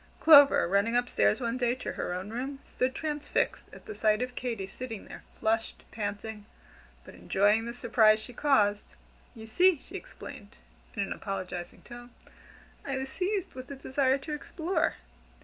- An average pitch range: Yes, average, 4.2 semitones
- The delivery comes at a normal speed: Yes, average, 165 wpm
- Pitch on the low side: No, high, 240 Hz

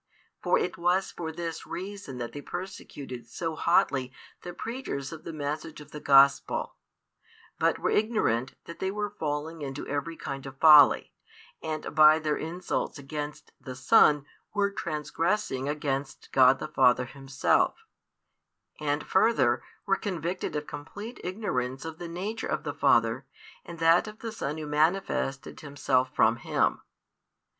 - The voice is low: No, medium, 150 Hz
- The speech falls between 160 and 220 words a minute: No, average, 150 wpm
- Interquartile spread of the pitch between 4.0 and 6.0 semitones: Yes, average, 4.4 semitones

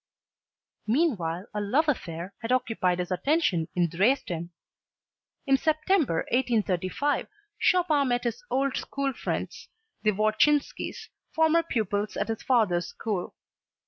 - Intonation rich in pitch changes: Yes, wide, 7.4 semitones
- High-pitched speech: Yes, high, 230 Hz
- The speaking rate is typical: No, slow, 115 wpm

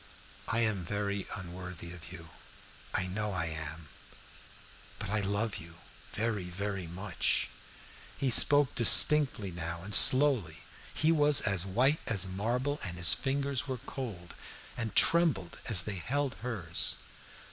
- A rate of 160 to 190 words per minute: No, average, 140 wpm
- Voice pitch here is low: Yes, low, 100 Hz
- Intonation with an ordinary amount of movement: No, wide, 6.2 semitones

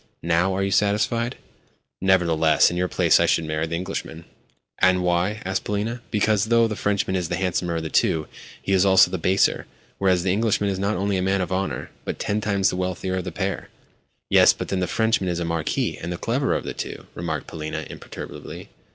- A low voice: Yes, very low, 95 Hz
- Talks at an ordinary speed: No, fast, 210 wpm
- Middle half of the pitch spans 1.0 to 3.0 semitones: Yes, average, 2.7 semitones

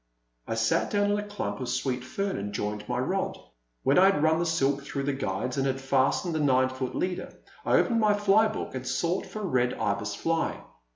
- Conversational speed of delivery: No, fast, 225 wpm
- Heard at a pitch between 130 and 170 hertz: Yes, medium, 140 Hz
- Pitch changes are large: Yes, wide, 6.9 semitones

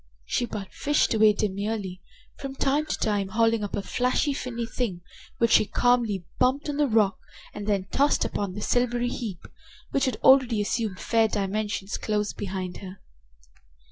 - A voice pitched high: Yes, high, 220 Hz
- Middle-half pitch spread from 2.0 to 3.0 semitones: No, average, 3.6 semitones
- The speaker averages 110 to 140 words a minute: No, average, 165 wpm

